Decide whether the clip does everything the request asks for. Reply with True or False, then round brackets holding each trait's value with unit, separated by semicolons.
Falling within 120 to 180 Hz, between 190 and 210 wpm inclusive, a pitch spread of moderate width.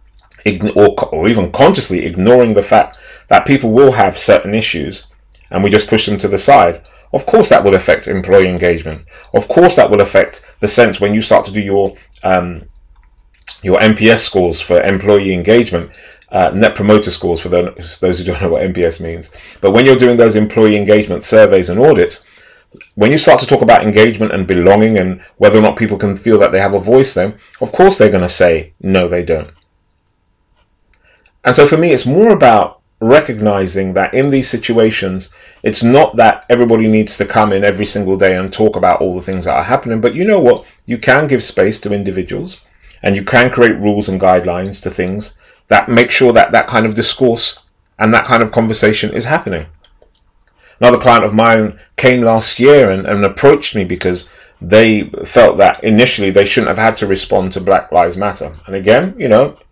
False (100 Hz; 200 wpm; 3.8 semitones)